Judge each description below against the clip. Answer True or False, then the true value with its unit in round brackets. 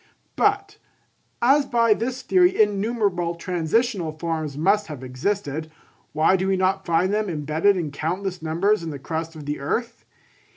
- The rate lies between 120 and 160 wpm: True (155 wpm)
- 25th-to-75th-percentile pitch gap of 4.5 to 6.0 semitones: True (5.2 semitones)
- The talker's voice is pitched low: False (185 Hz)